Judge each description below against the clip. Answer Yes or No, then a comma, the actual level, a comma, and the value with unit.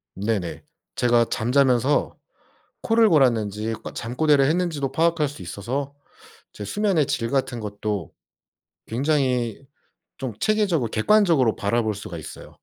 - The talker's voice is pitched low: Yes, low, 125 Hz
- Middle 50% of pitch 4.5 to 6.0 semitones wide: Yes, wide, 5.4 semitones